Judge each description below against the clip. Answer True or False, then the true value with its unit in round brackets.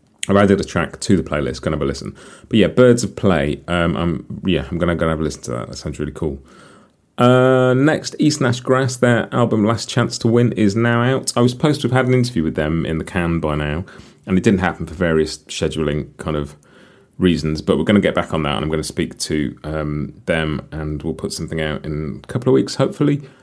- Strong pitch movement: True (7.8 semitones)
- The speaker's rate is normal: False (245 wpm)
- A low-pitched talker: True (90 Hz)